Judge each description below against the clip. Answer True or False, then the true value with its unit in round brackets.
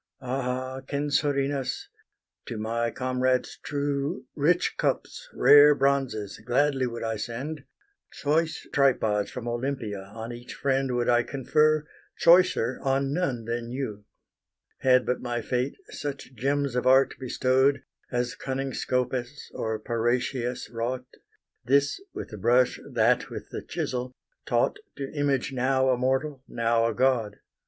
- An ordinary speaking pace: False (130 wpm)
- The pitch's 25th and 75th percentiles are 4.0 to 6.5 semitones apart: False (2.6 semitones)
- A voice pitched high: False (130 Hz)